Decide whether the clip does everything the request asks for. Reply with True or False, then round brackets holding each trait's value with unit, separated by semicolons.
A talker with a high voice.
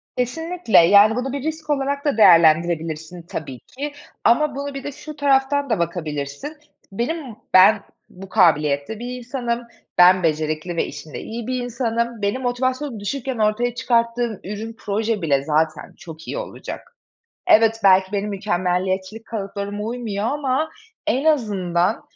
True (220 Hz)